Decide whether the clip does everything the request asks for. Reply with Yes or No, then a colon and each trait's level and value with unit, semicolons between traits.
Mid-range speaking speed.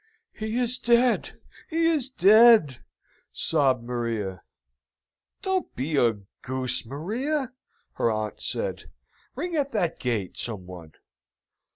No: slow, 110 wpm